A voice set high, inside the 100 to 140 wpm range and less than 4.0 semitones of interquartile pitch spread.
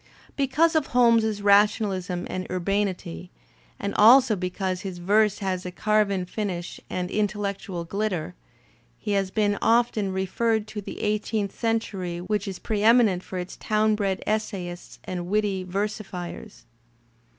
Yes: high, 200 Hz; slow, 135 wpm; average, 2.7 semitones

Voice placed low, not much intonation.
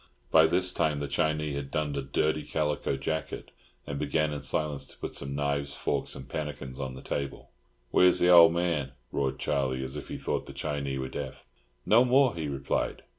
Yes: very low, 75 Hz; narrow, 2.3 semitones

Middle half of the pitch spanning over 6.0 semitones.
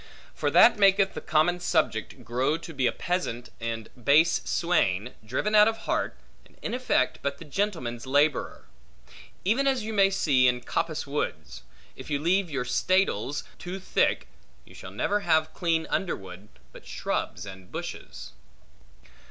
Yes: wide, 7.5 semitones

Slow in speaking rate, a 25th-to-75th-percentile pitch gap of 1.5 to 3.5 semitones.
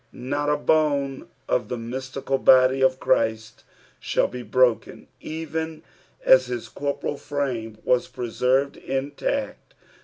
Yes: slow, 120 wpm; narrow, 2.5 semitones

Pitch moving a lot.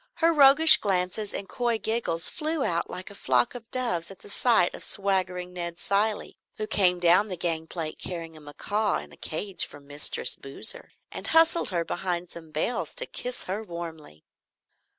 No: average, 4.6 semitones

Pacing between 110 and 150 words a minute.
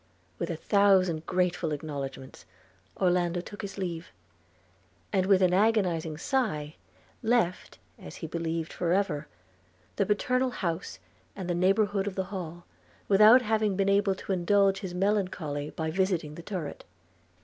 Yes: average, 140 wpm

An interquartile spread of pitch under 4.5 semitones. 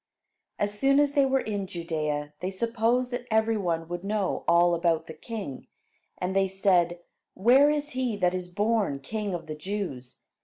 No: average, 4.9 semitones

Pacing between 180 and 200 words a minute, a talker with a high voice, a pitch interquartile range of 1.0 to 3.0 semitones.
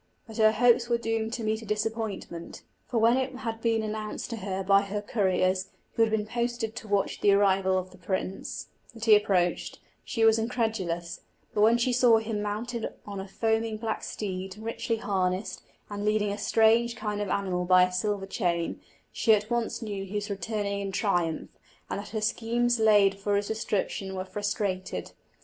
Yes: average, 190 wpm; high, 210 Hz; narrow, 2.5 semitones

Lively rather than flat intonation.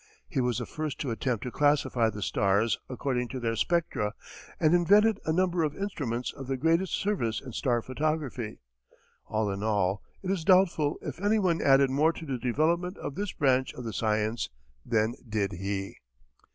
Yes: wide, 6.5 semitones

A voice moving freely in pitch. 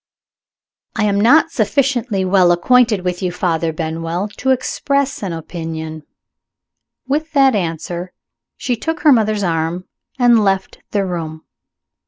Yes: wide, 6.4 semitones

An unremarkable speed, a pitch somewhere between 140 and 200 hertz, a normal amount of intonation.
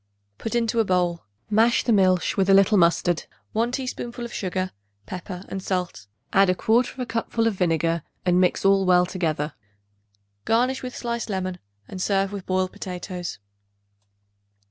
Yes: average, 145 wpm; high, 190 Hz; average, 3.9 semitones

